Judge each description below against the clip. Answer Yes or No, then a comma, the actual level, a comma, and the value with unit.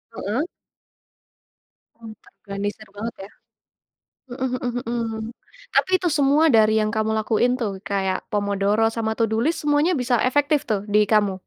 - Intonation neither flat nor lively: Yes, average, 3.2 semitones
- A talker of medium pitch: No, high, 225 Hz